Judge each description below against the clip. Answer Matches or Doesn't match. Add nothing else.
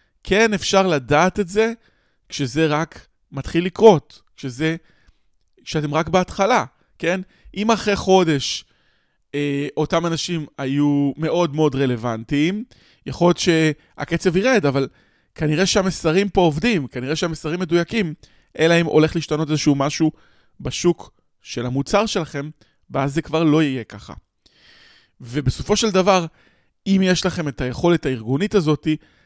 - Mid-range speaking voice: Matches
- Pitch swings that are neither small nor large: Matches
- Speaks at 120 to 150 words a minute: Matches